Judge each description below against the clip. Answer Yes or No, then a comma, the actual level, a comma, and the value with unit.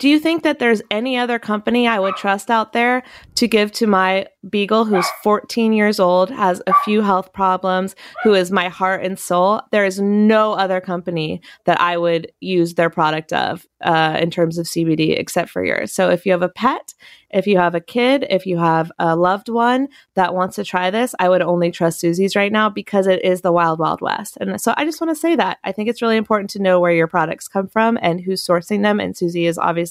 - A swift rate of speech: Yes, fast, 235 wpm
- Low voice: No, high, 190 Hz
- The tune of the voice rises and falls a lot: No, average, 3.6 semitones